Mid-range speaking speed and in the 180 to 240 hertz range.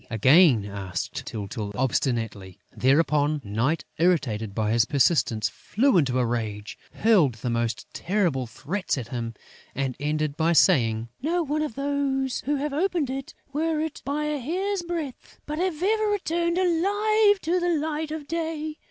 Yes: average, 155 wpm; medium, 185 Hz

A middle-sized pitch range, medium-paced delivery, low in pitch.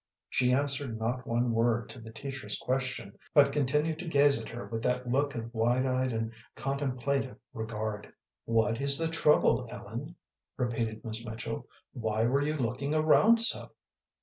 Yes: average, 3.6 semitones; average, 160 wpm; low, 125 Hz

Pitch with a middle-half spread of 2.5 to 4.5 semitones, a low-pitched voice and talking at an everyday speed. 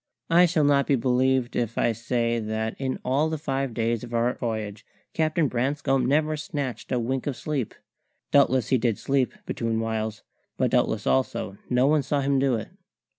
Yes: average, 3.3 semitones; low, 130 Hz; average, 180 wpm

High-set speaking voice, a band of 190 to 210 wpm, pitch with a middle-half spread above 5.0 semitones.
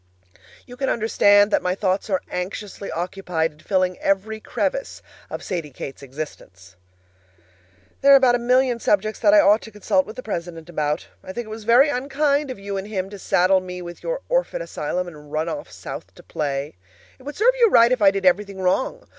Yes: high, 200 Hz; average, 200 wpm; wide, 5.6 semitones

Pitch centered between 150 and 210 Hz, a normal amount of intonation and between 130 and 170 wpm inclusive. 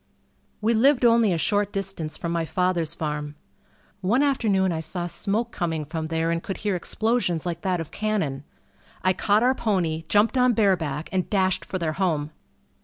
No: medium, 185 Hz; average, 4.6 semitones; average, 180 wpm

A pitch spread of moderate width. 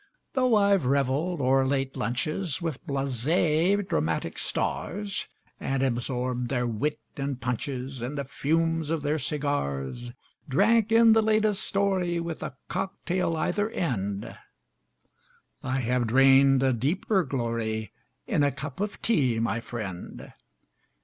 No: wide, 5.8 semitones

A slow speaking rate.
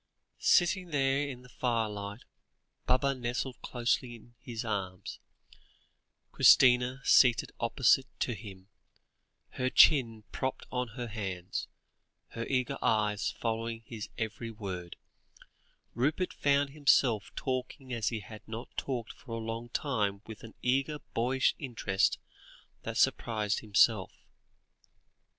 Yes: slow, 120 wpm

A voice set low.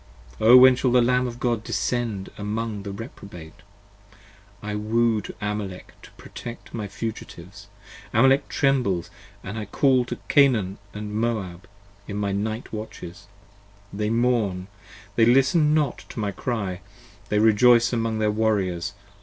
Yes: low, 110 Hz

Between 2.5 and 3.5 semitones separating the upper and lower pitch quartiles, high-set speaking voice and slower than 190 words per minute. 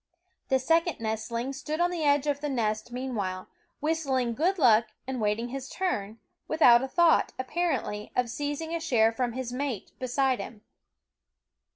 No: average, 4.4 semitones; very high, 260 Hz; average, 160 wpm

